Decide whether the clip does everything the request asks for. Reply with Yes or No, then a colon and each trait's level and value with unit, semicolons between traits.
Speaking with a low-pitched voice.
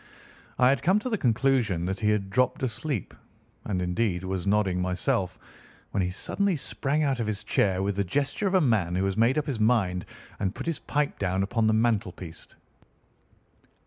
Yes: low, 110 Hz